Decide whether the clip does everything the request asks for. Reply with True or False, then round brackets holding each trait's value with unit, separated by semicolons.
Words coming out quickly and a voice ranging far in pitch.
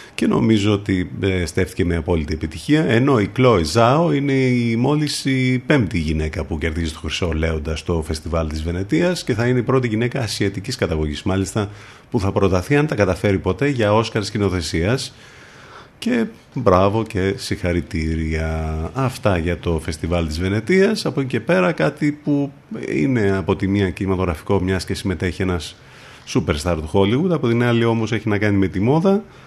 True (175 wpm; 6.5 semitones)